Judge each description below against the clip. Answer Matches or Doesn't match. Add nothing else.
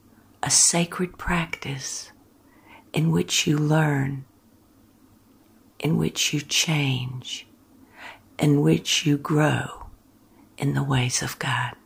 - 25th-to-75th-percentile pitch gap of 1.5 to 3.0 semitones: Matches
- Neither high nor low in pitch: Matches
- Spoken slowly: Matches